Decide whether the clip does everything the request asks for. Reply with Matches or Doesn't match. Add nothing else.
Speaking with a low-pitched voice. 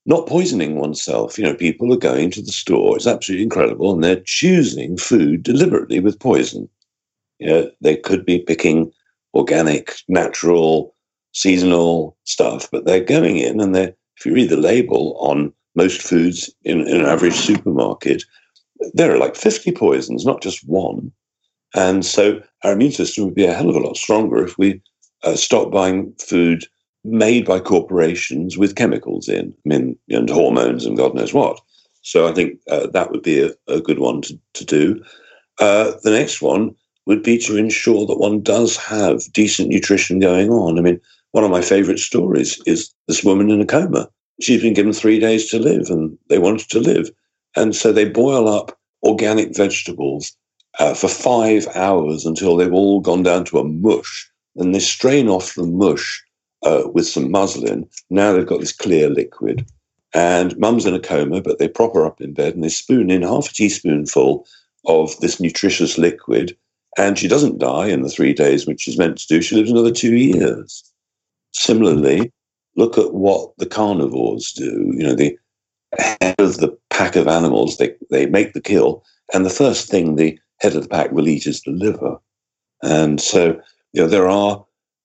Matches